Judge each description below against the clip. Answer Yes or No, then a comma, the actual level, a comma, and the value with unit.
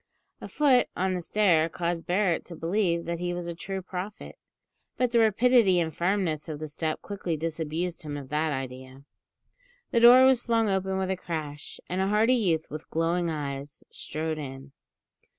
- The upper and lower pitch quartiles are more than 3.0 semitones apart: Yes, average, 3.9 semitones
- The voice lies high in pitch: No, medium, 170 Hz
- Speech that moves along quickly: No, average, 180 wpm